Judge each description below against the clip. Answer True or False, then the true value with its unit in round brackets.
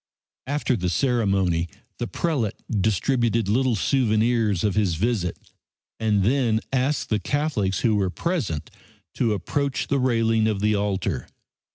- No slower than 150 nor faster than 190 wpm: False (135 wpm)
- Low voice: True (110 Hz)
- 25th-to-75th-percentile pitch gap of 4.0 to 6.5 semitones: True (4.3 semitones)